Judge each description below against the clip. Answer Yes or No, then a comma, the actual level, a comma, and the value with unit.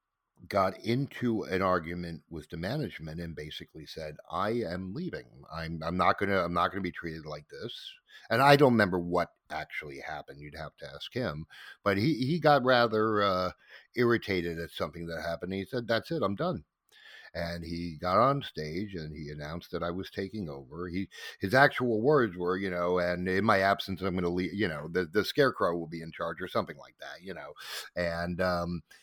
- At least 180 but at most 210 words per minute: Yes, average, 200 wpm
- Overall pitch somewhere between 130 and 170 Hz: No, very low, 90 Hz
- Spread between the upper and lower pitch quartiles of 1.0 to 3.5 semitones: No, average, 4.1 semitones